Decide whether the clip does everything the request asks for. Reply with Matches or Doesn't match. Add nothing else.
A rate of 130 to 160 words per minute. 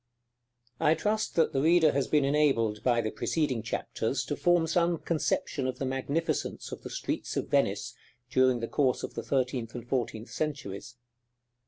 Doesn't match